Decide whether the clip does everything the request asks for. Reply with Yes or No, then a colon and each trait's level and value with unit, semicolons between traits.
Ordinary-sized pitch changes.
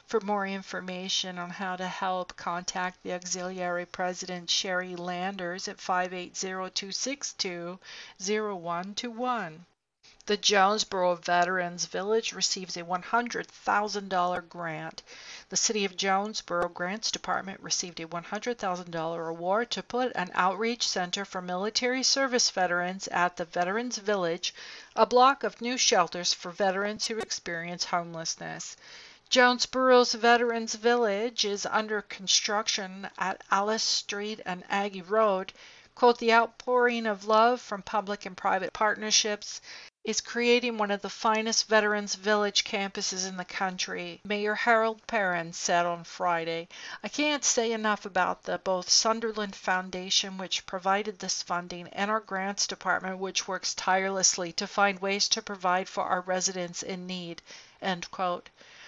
Yes: average, 3.2 semitones